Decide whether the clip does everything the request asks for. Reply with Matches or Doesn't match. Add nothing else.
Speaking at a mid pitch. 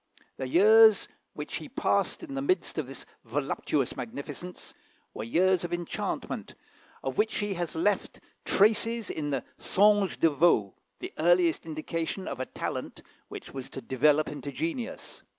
Matches